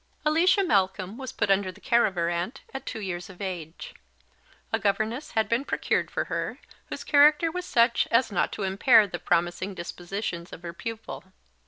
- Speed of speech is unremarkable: Yes, average, 185 wpm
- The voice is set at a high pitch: Yes, high, 200 Hz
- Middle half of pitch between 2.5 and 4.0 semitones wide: No, wide, 5.5 semitones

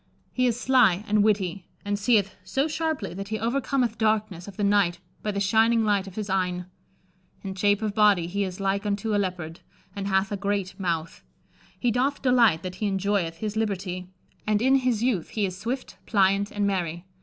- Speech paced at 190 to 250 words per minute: Yes, average, 195 wpm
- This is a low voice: No, high, 205 Hz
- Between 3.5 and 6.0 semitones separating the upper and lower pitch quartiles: No, average, 2.7 semitones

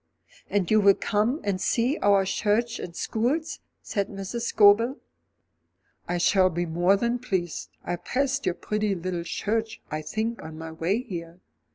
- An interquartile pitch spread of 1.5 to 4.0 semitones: No, average, 4.7 semitones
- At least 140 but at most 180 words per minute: Yes, average, 160 wpm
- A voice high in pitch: Yes, high, 205 Hz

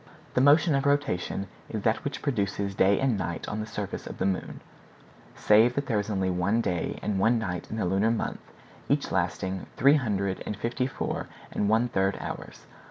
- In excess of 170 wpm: Yes, average, 195 wpm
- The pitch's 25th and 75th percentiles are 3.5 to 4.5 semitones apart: Yes, average, 4.2 semitones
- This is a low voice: Yes, low, 105 Hz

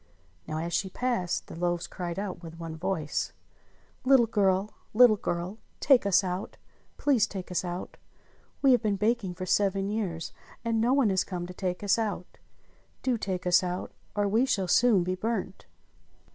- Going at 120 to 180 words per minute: Yes, average, 175 wpm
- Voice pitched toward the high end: Yes, high, 195 Hz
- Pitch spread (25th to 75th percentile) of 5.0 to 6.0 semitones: No, average, 3.8 semitones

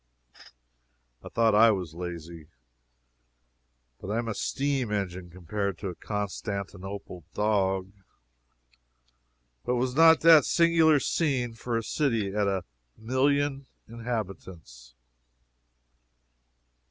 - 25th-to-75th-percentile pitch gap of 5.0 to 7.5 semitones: Yes, average, 5.3 semitones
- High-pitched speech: No, low, 105 Hz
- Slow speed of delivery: Yes, slow, 105 wpm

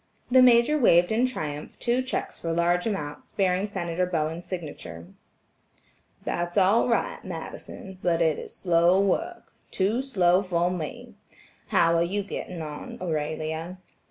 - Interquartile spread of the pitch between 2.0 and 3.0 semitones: No, average, 3.7 semitones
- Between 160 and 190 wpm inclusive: No, slow, 135 wpm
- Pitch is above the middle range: No, medium, 180 Hz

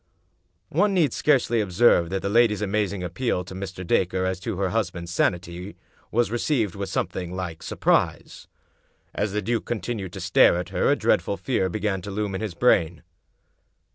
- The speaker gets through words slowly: No, average, 175 wpm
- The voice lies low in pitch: Yes, very low, 95 Hz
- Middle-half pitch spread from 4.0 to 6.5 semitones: No, average, 3.3 semitones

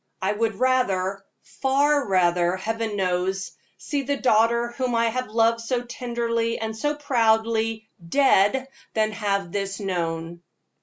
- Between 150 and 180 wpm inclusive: No, slow, 135 wpm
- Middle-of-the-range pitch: No, high, 225 Hz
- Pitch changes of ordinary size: Yes, average, 3.7 semitones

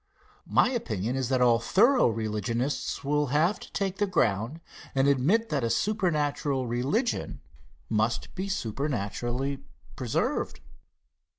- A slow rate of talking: Yes, slow, 120 wpm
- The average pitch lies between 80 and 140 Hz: Yes, low, 135 Hz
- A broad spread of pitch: Yes, wide, 7.0 semitones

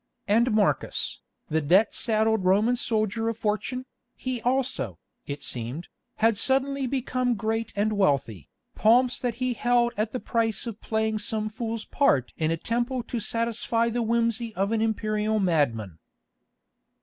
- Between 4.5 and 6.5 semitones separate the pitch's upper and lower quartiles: No, average, 2.7 semitones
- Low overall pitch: No, high, 220 Hz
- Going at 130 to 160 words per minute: Yes, average, 150 wpm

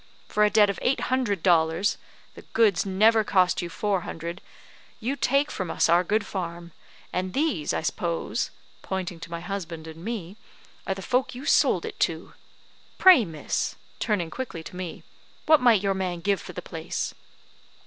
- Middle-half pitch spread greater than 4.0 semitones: Yes, average, 4.5 semitones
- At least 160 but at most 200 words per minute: Yes, average, 175 wpm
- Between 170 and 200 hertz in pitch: Yes, high, 190 Hz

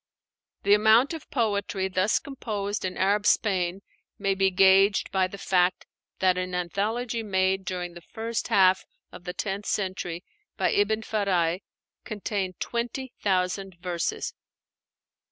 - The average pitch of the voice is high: Yes, high, 195 Hz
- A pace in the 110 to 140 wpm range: Yes, slow, 135 wpm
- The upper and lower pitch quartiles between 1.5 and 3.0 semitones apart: Yes, narrow, 2.4 semitones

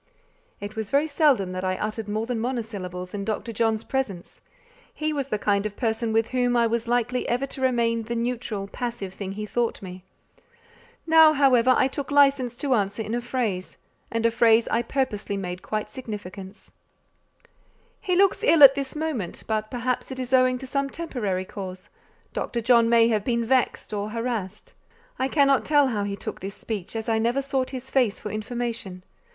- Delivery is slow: No, average, 190 wpm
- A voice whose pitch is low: No, high, 230 Hz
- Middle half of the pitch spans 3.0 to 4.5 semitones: Yes, average, 3.7 semitones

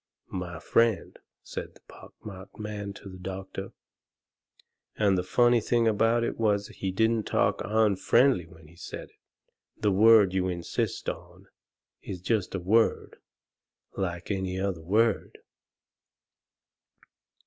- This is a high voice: No, low, 100 Hz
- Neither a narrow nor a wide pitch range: Yes, average, 3.2 semitones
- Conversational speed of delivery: No, slow, 130 wpm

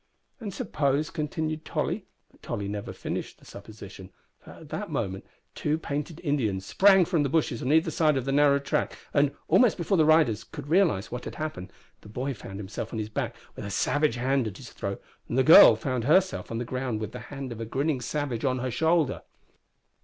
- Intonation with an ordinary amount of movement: No, wide, 5.7 semitones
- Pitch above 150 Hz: No, low, 135 Hz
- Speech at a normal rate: No, fast, 210 wpm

